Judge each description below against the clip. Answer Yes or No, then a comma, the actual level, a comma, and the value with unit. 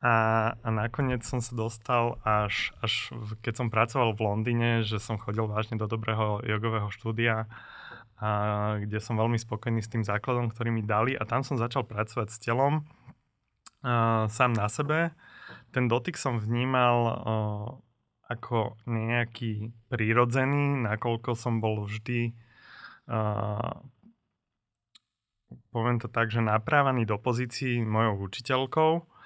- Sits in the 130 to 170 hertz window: No, low, 115 Hz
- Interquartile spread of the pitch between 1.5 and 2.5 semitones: Yes, narrow, 1.9 semitones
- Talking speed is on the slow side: No, average, 135 wpm